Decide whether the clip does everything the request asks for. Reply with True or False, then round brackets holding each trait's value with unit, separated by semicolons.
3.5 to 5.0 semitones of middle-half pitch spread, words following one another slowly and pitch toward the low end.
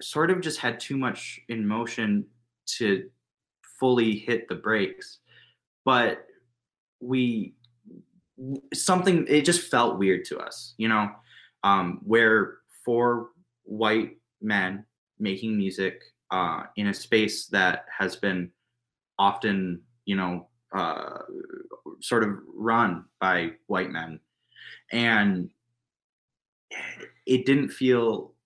True (4.2 semitones; 110 wpm; 115 Hz)